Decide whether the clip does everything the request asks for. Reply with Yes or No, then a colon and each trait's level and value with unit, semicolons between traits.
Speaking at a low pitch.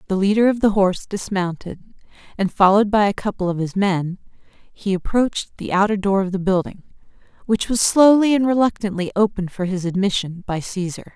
No: high, 200 Hz